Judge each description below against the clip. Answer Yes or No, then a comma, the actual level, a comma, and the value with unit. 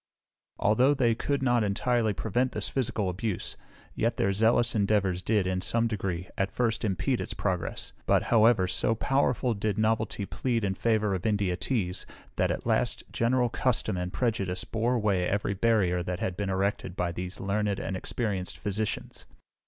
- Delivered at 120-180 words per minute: Yes, average, 170 wpm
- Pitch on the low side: Yes, low, 105 Hz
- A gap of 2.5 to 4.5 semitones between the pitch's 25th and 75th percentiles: Yes, average, 3.5 semitones